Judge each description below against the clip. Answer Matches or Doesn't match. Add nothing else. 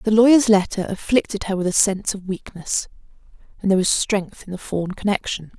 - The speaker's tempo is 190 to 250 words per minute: Matches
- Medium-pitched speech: Doesn't match